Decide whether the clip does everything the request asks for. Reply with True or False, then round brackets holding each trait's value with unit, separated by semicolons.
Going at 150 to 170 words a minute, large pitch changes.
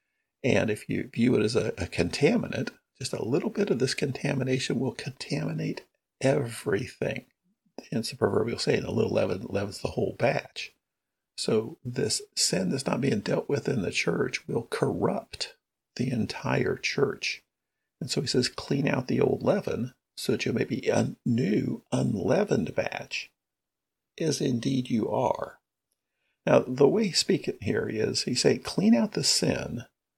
True (165 wpm; 8.6 semitones)